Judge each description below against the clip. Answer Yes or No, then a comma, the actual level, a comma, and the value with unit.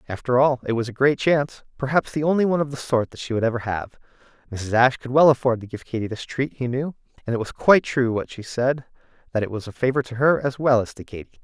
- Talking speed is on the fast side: Yes, fast, 260 wpm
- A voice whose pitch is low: Yes, low, 125 Hz